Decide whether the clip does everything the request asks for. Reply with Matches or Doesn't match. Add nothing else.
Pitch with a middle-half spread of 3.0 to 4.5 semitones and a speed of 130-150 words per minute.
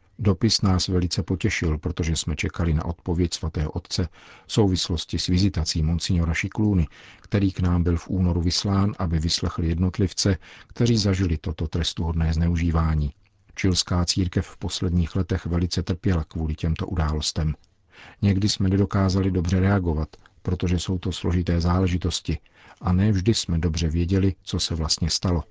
Doesn't match